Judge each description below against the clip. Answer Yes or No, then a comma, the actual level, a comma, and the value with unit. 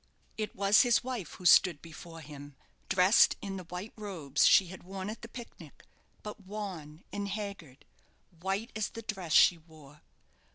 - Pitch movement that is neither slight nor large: Yes, average, 4.4 semitones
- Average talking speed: Yes, average, 165 wpm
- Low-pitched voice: No, high, 190 Hz